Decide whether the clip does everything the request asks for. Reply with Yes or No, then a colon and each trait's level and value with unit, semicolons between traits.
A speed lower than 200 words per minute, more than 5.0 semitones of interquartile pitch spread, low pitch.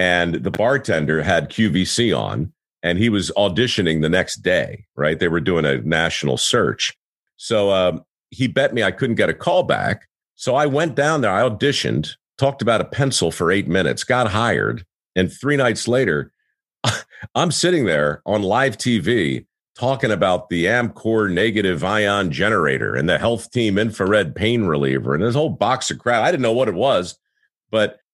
Yes: average, 180 wpm; wide, 5.6 semitones; low, 100 Hz